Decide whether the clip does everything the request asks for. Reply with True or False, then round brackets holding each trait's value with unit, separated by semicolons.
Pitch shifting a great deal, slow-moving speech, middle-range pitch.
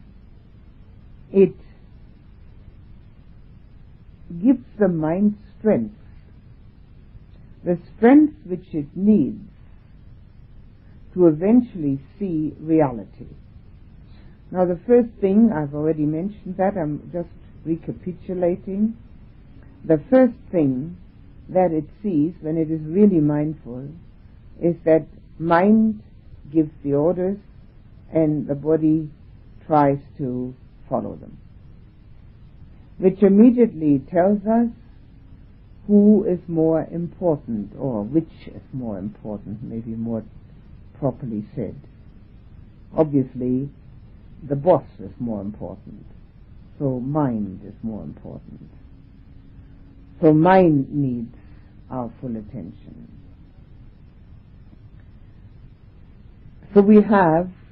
True (8.4 semitones; 90 wpm; 145 Hz)